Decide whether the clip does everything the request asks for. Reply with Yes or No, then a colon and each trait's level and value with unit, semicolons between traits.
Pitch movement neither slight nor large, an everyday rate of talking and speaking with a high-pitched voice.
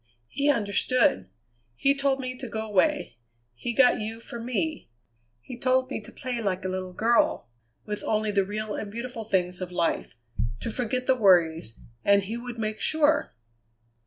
Yes: average, 4.3 semitones; average, 170 wpm; high, 225 Hz